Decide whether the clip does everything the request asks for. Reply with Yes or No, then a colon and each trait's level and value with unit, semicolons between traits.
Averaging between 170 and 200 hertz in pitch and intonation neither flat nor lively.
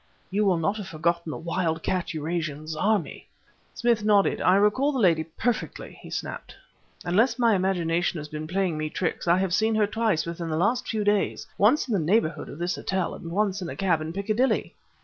Yes: medium, 185 Hz; average, 4.2 semitones